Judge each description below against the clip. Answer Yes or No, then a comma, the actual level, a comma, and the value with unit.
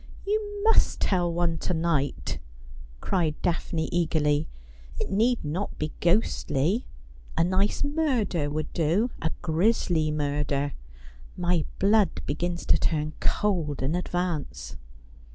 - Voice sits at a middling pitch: Yes, medium, 170 Hz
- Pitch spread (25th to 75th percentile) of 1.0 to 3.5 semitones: No, average, 4.5 semitones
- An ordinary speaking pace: No, slow, 130 wpm